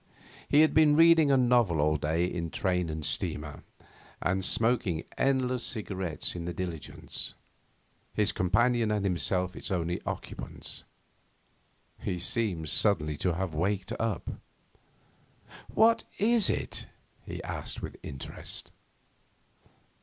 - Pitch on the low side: Yes, very low, 95 Hz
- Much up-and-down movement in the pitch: Yes, wide, 6.4 semitones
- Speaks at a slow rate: Yes, slow, 120 wpm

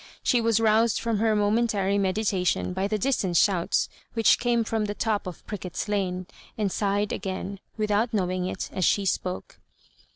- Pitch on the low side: No, high, 205 Hz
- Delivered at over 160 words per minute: Yes, average, 170 wpm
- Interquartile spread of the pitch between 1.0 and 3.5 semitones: Yes, average, 2.8 semitones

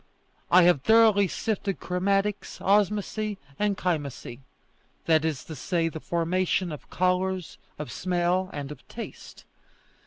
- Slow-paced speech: Yes, slow, 125 wpm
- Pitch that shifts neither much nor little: Yes, average, 3.4 semitones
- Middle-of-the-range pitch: Yes, medium, 180 Hz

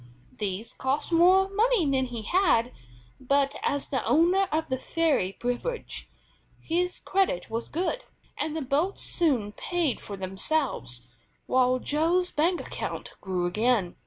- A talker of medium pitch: No, very high, 285 Hz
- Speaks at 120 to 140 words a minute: Yes, slow, 135 wpm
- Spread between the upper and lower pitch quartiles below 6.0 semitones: No, wide, 7.0 semitones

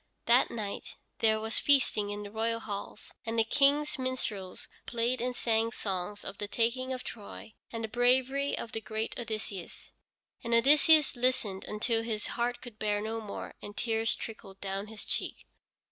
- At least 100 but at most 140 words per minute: No, average, 175 wpm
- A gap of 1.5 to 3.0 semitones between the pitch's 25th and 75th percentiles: Yes, average, 2.7 semitones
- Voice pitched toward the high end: Yes, high, 225 Hz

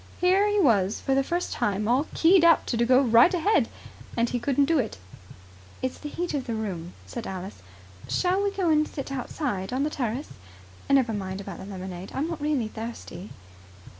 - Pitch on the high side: Yes, very high, 255 Hz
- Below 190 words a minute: No, average, 195 wpm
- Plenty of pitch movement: Yes, wide, 6.7 semitones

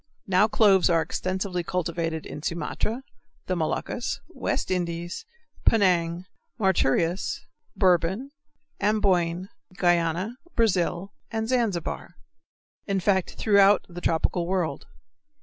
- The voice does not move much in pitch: No, average, 3.0 semitones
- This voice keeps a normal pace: No, slow, 95 wpm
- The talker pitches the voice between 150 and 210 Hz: Yes, medium, 185 Hz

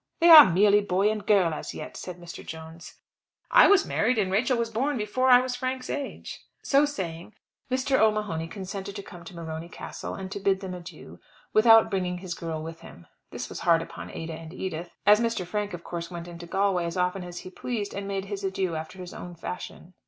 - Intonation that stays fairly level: No, average, 3.9 semitones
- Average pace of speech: No, fast, 210 wpm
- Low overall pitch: No, high, 190 Hz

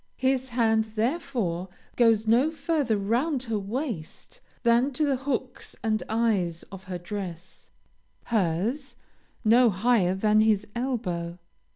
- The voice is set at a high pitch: Yes, high, 225 Hz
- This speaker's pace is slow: Yes, slow, 130 wpm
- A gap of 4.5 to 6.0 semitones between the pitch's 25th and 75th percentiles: Yes, average, 4.8 semitones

